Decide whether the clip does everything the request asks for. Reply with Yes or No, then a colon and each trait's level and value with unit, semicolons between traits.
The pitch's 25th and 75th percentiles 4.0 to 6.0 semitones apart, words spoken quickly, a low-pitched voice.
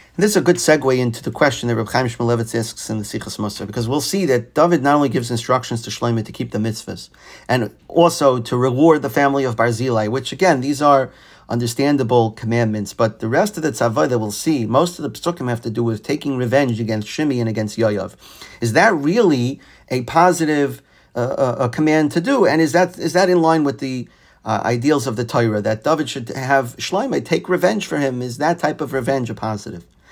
Yes: average, 4.3 semitones; fast, 220 wpm; low, 130 Hz